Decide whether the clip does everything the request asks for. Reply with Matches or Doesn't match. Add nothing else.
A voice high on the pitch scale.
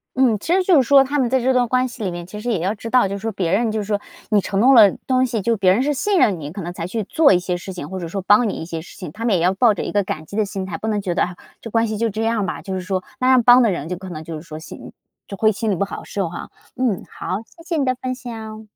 Matches